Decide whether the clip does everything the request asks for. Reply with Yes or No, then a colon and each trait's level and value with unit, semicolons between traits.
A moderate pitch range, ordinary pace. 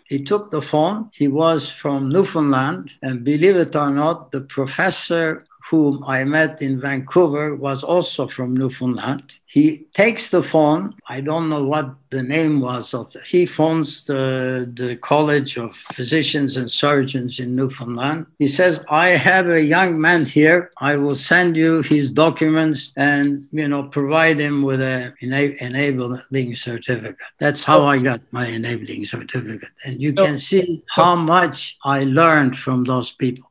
Yes: average, 3.4 semitones; average, 160 wpm